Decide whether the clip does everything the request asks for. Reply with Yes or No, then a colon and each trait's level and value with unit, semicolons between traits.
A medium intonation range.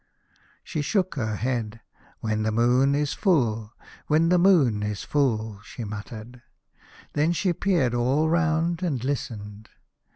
No: wide, 6.5 semitones